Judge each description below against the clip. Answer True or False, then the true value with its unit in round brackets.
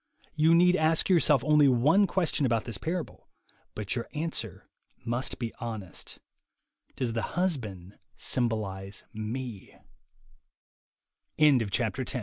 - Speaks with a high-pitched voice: False (125 Hz)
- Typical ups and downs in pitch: False (6.4 semitones)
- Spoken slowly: True (100 wpm)